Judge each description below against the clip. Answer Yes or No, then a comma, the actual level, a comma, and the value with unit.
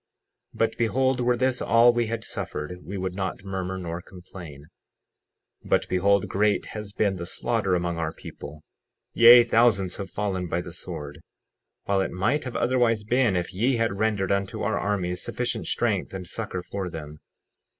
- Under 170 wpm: No, average, 175 wpm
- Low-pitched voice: Yes, low, 100 Hz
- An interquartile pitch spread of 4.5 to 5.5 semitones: No, average, 4.1 semitones